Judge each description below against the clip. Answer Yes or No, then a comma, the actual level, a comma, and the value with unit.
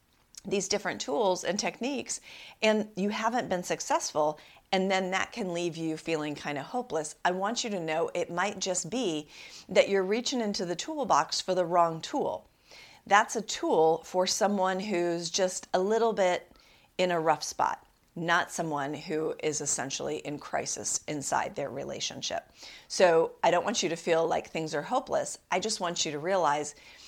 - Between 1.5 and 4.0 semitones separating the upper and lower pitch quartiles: Yes, average, 3.7 semitones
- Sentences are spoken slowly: No, average, 175 wpm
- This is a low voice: No, medium, 180 Hz